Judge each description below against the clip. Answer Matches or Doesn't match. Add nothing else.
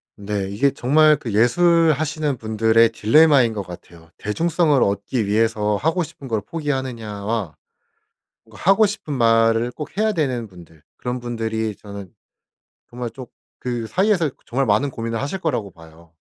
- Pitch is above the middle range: Doesn't match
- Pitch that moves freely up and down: Matches